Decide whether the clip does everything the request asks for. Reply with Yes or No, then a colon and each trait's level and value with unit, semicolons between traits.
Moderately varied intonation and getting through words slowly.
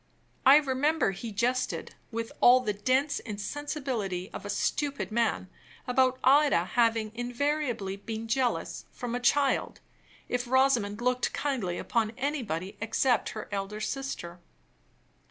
Yes: average, 4.1 semitones; slow, 125 wpm